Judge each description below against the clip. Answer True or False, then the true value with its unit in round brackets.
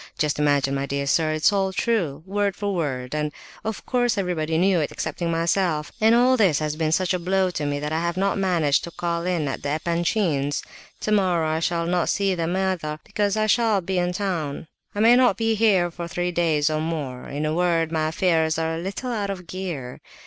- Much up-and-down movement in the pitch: False (3.8 semitones)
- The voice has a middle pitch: True (170 Hz)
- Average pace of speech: False (215 wpm)